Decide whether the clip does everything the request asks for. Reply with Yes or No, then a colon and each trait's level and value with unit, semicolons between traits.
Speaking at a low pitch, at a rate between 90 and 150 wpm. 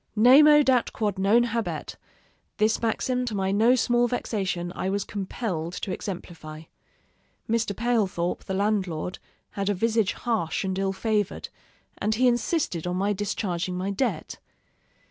No: high, 205 Hz; average, 145 wpm